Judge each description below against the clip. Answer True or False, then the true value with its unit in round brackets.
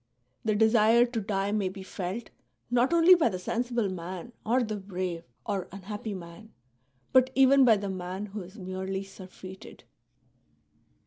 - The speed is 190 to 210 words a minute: False (150 wpm)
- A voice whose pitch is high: True (205 Hz)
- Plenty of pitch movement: False (3.7 semitones)